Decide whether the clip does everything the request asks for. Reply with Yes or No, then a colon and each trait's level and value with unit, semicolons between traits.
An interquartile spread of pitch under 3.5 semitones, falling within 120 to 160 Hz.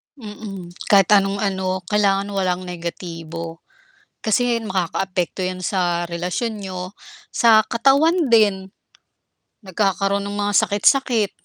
No: narrow, 2.6 semitones; high, 195 Hz